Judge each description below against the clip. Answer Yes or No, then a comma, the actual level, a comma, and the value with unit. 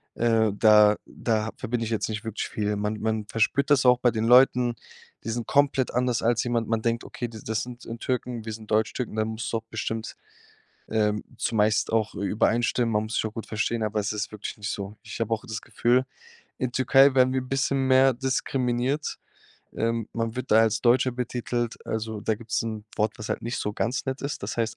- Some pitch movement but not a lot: No, narrow, 2.3 semitones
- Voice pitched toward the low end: Yes, low, 115 Hz